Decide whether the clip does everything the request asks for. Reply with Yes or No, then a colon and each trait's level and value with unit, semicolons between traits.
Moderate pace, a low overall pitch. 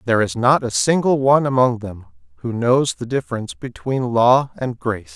Yes: average, 185 wpm; low, 125 Hz